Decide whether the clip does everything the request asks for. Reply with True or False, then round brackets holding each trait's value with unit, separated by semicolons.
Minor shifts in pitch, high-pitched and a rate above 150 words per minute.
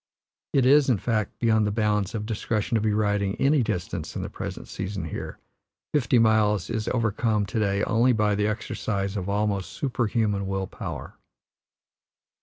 False (2.2 semitones; 105 Hz; 165 wpm)